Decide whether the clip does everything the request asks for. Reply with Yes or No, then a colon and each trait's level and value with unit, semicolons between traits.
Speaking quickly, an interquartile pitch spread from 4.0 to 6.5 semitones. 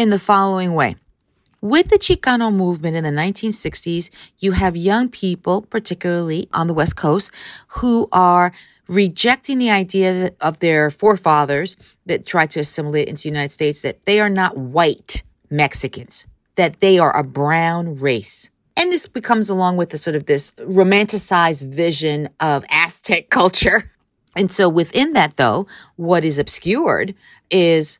No: average, 150 wpm; average, 4.7 semitones